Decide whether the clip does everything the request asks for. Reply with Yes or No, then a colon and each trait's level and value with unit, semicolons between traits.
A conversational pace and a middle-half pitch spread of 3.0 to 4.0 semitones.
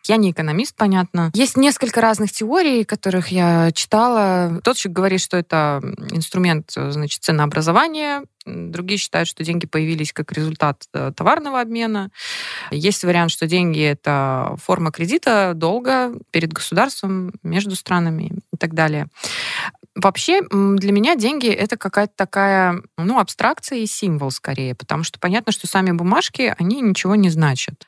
No: average, 140 wpm; average, 4.6 semitones